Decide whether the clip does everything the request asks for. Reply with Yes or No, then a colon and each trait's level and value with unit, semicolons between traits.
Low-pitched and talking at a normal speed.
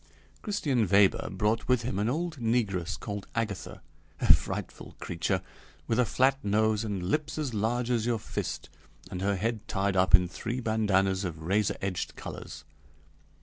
Yes: low, 105 Hz; average, 160 wpm